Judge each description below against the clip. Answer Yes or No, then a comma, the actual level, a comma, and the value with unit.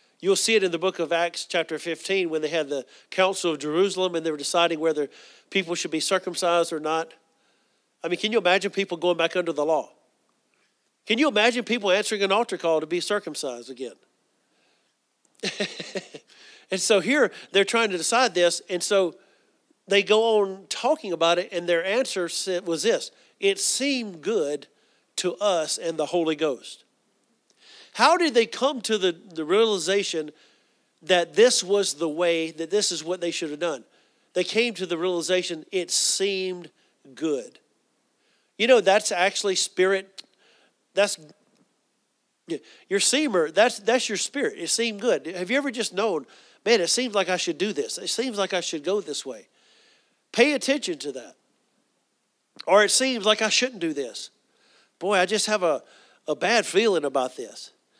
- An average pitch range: Yes, average, 4.3 semitones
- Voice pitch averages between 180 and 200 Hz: Yes, high, 190 Hz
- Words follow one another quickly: No, average, 175 wpm